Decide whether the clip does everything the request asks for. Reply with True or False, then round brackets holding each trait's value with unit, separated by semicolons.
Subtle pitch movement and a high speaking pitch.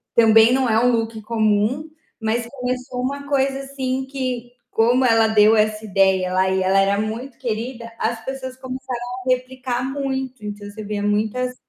False (3.3 semitones; 240 Hz)